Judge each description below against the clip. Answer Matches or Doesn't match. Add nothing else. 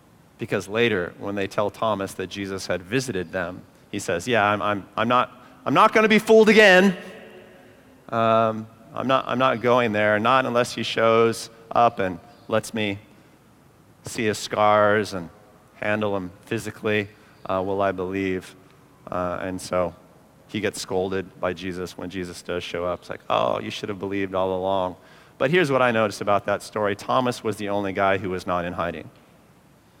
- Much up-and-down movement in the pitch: Doesn't match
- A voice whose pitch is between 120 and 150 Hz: Doesn't match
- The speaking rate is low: Doesn't match